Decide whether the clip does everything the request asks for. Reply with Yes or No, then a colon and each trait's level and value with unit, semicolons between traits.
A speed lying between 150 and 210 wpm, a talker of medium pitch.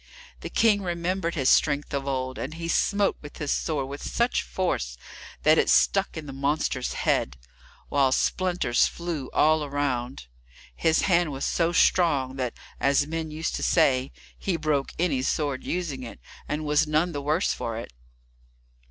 Yes: average, 170 wpm; medium, 150 Hz